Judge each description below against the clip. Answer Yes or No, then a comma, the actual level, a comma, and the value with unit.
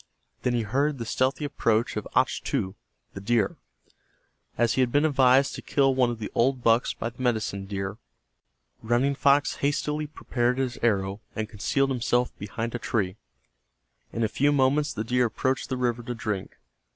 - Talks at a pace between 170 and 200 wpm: Yes, average, 175 wpm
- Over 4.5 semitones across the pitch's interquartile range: No, average, 3.3 semitones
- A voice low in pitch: Yes, low, 120 Hz